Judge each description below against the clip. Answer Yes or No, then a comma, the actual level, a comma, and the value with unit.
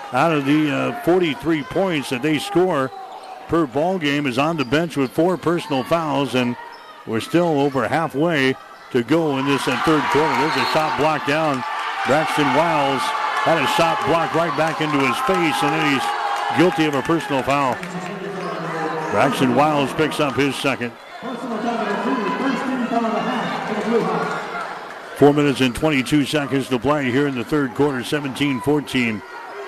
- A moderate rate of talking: Yes, average, 150 wpm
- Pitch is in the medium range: Yes, medium, 150 Hz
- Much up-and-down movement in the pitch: No, average, 4.1 semitones